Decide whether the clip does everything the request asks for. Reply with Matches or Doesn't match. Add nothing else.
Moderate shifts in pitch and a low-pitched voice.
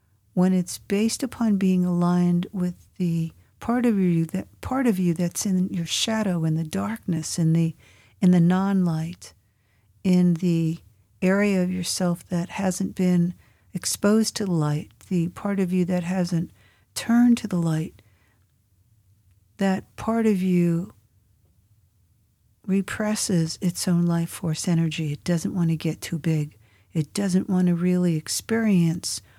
Doesn't match